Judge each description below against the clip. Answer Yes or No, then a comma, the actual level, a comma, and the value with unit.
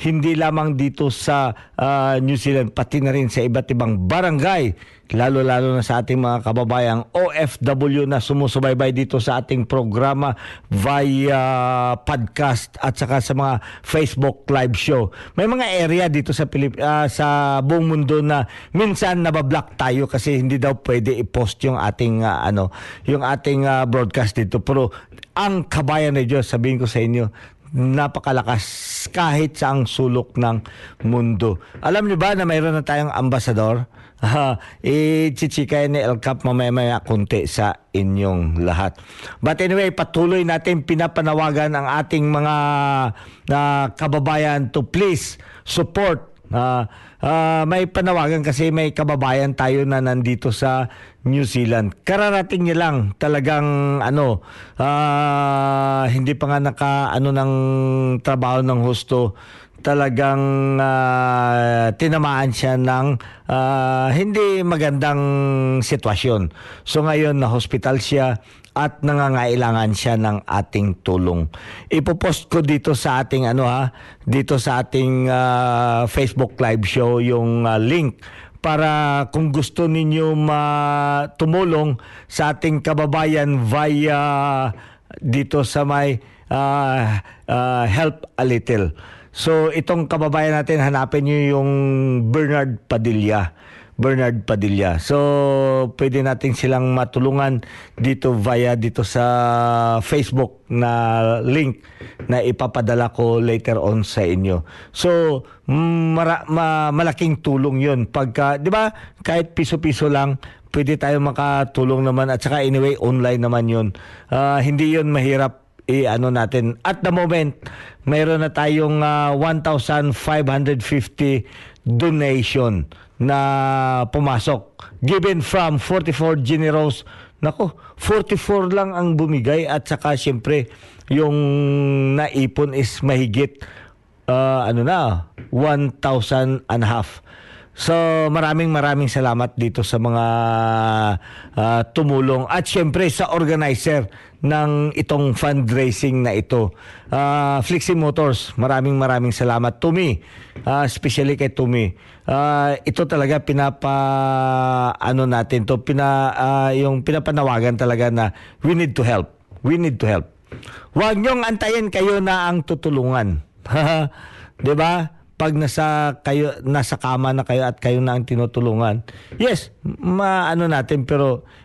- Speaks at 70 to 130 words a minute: Yes, average, 125 wpm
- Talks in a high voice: No, low, 135 Hz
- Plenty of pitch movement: No, average, 3.7 semitones